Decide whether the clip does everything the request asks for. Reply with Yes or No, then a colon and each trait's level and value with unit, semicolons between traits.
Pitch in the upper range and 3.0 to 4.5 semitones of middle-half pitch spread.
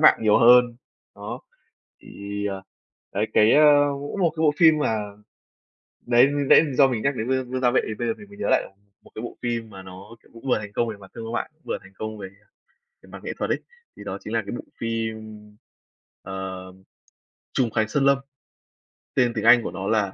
No: low, 115 Hz; average, 4.0 semitones